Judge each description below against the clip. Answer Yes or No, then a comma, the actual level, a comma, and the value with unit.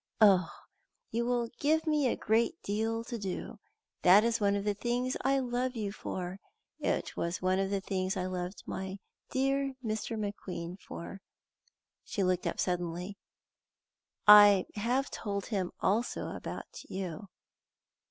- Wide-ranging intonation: No, average, 4.0 semitones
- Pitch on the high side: Yes, high, 205 Hz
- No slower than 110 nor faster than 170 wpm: Yes, average, 145 wpm